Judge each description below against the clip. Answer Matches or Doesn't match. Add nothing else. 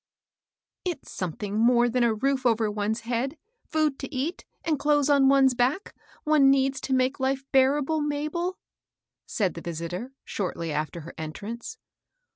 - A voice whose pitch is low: Doesn't match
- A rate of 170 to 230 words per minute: Doesn't match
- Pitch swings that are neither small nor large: Matches